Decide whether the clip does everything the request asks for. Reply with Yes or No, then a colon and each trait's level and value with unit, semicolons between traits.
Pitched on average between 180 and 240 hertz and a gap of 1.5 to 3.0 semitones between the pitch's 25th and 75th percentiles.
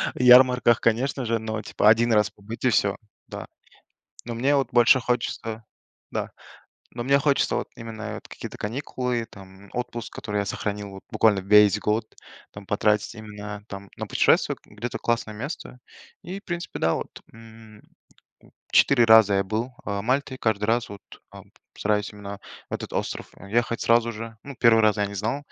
No: low, 110 Hz; average, 2.7 semitones